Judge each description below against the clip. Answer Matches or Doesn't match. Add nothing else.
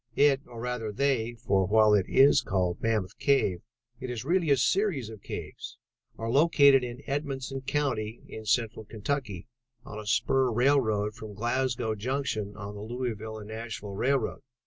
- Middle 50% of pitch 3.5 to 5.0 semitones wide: Matches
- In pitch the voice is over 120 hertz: Doesn't match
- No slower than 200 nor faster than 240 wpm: Doesn't match